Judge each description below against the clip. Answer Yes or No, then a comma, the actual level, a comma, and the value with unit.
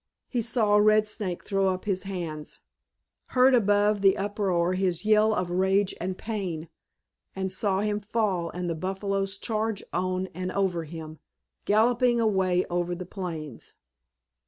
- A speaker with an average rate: Yes, average, 145 wpm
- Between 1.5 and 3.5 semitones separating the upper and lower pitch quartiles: Yes, average, 2.9 semitones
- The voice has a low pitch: No, high, 195 Hz